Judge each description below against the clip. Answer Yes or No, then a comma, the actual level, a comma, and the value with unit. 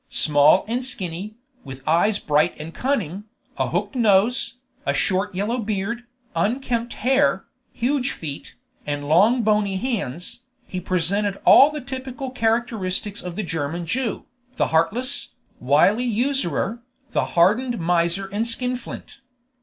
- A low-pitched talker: No, high, 205 Hz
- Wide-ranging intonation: Yes, wide, 6.0 semitones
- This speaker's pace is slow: Yes, slow, 130 wpm